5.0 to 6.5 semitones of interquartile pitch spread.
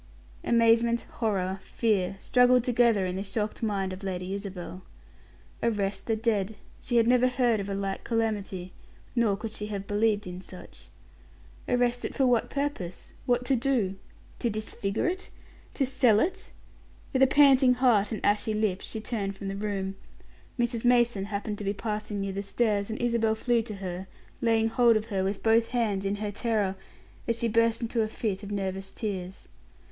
No: average, 3.1 semitones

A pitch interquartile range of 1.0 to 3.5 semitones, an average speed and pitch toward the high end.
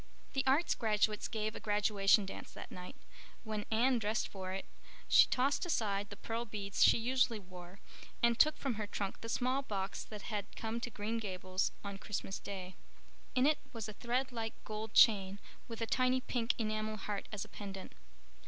Yes: average, 2.9 semitones; average, 185 wpm; high, 215 Hz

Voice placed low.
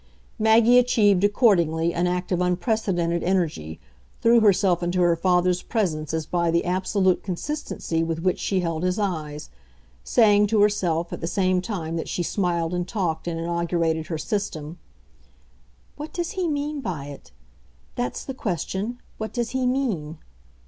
No: medium, 180 Hz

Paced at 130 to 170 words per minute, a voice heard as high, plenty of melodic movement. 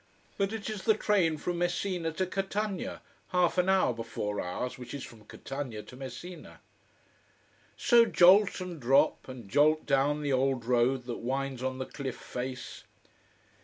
No: average, 160 wpm; medium, 140 Hz; wide, 6.3 semitones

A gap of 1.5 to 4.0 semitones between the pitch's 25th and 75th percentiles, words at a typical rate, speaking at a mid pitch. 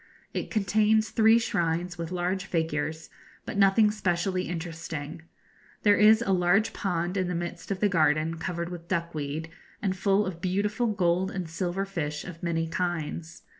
Yes: average, 3.0 semitones; average, 160 wpm; medium, 180 Hz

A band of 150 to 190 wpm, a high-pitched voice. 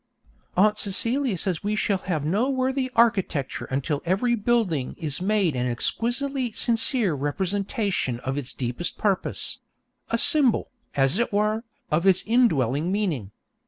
No: slow, 135 wpm; high, 200 Hz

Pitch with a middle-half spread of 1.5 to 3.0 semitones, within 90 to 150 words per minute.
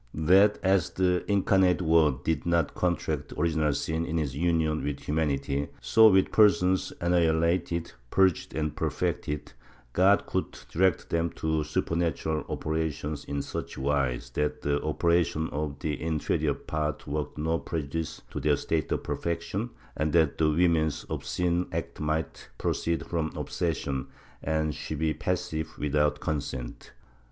Yes: narrow, 2.4 semitones; average, 140 wpm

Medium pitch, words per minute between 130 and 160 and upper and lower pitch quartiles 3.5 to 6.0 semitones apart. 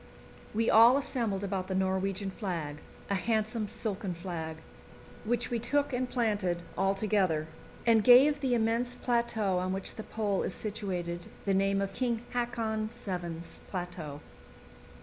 No: high, 205 Hz; average, 145 wpm; average, 4.0 semitones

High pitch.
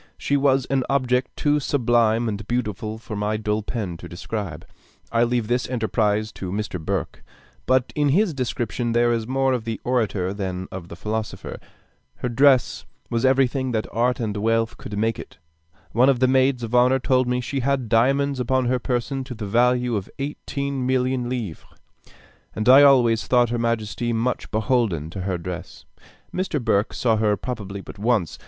No: low, 120 Hz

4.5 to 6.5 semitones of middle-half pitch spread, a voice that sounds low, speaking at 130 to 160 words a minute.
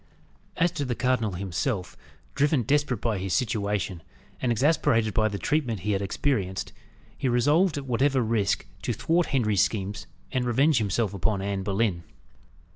Yes: average, 5.2 semitones; low, 115 Hz; average, 155 wpm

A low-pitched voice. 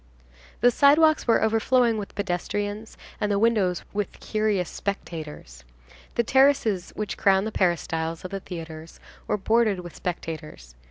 No: high, 200 Hz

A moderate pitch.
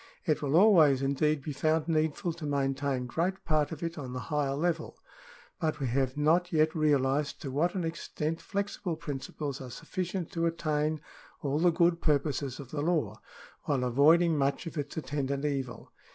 Yes: medium, 150 Hz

